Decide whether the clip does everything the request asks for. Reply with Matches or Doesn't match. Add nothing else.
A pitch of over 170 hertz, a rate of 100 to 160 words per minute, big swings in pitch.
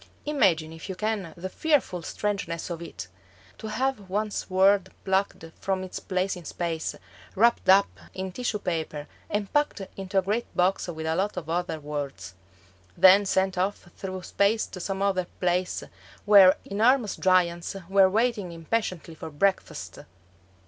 Doesn't match